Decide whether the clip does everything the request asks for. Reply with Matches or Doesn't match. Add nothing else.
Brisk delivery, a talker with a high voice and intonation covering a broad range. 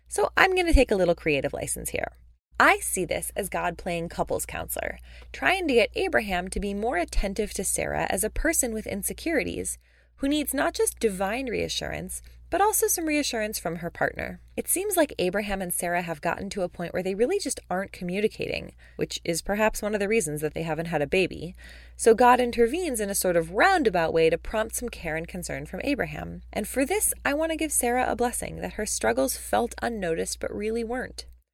Matches